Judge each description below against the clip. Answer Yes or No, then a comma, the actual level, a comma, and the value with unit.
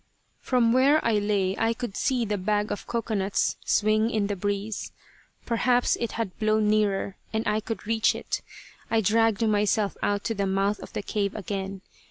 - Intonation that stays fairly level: Yes, narrow, 2.0 semitones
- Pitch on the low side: No, high, 215 Hz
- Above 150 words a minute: Yes, average, 180 wpm